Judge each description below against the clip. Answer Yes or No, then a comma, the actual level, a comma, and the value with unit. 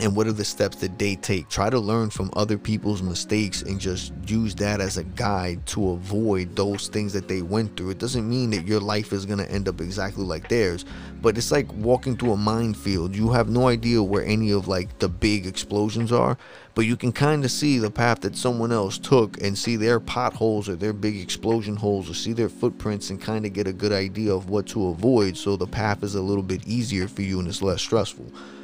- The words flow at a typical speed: No, fast, 235 wpm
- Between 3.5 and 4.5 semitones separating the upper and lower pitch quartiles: No, average, 2.8 semitones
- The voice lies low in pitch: Yes, low, 105 Hz